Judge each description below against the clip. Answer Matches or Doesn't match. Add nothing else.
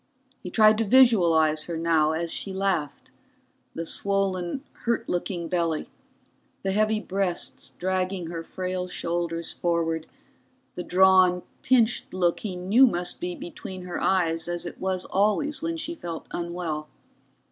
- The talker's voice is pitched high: Doesn't match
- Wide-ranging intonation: Doesn't match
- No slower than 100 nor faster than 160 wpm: Matches